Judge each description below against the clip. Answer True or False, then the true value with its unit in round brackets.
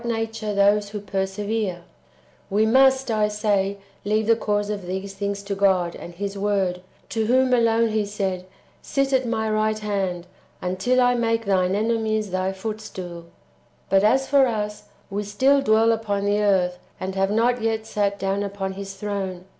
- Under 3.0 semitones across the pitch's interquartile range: True (2.4 semitones)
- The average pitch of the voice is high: True (205 Hz)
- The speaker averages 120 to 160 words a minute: False (175 wpm)